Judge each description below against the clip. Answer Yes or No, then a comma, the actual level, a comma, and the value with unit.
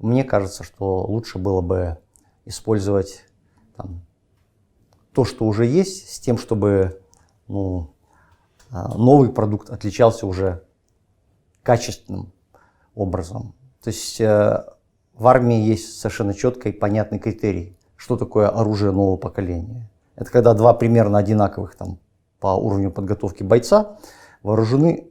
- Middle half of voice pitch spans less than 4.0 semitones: Yes, average, 3.2 semitones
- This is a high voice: No, low, 105 Hz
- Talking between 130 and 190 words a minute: No, average, 115 wpm